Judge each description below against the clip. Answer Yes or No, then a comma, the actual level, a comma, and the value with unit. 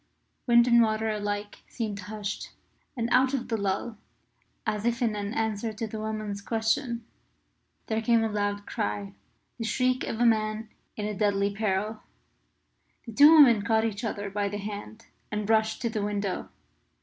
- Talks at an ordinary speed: Yes, average, 160 wpm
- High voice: Yes, high, 215 Hz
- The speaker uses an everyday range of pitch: No, narrow, 1.9 semitones